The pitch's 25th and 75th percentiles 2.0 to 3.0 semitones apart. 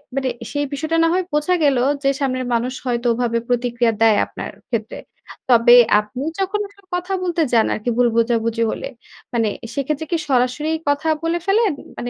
No: average, 5.2 semitones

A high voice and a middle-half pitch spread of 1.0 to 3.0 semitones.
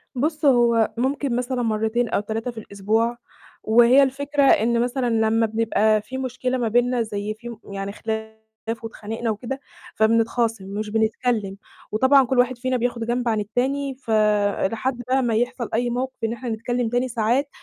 Yes: high, 235 Hz; narrow, 2.4 semitones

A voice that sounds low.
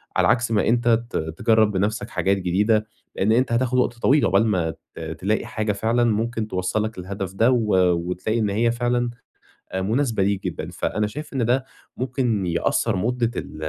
Yes: low, 110 Hz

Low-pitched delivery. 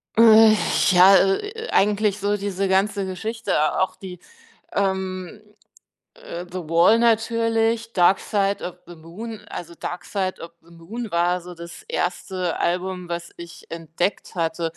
No: high, 190 Hz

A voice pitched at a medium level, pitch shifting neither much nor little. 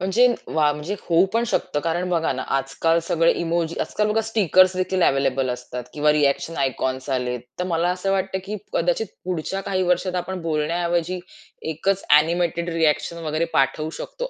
Yes: medium, 170 Hz; average, 3.6 semitones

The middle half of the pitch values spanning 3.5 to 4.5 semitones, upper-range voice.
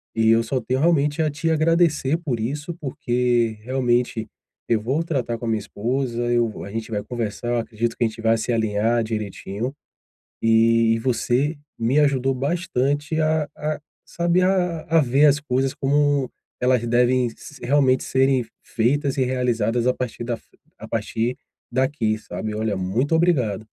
No: average, 4.1 semitones; low, 125 Hz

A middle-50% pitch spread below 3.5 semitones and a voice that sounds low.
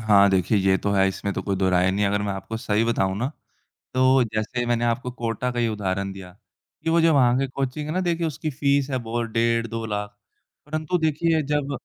No: average, 5.3 semitones; low, 115 Hz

